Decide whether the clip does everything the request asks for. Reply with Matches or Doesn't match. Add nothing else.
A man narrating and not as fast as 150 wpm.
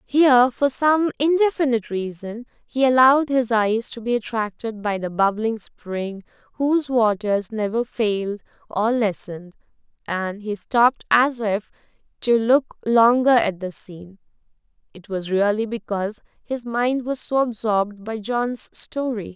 Doesn't match